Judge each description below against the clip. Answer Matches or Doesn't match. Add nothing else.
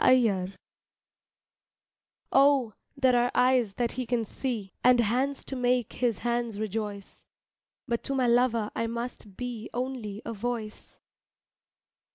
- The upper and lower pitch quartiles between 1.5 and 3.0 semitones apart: Matches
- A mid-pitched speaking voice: Doesn't match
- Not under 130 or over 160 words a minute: Matches